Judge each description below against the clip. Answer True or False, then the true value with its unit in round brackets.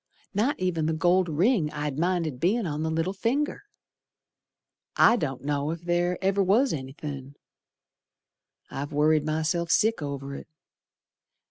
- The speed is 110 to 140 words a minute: True (135 wpm)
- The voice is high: False (160 Hz)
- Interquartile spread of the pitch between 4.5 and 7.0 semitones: False (4.0 semitones)